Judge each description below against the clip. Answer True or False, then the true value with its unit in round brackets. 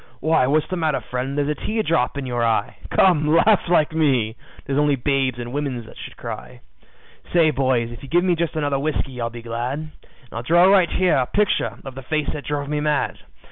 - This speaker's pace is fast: True (220 wpm)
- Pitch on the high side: False (145 Hz)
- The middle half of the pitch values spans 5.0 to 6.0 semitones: False (3.8 semitones)